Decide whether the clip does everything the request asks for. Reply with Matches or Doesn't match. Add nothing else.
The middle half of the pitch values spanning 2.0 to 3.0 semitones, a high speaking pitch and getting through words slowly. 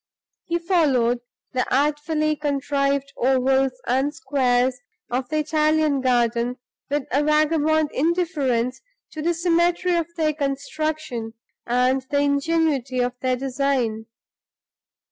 Doesn't match